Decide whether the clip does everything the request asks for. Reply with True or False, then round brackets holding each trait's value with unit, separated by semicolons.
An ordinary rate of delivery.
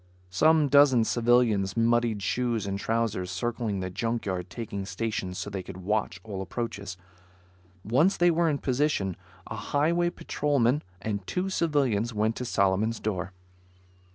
True (145 wpm)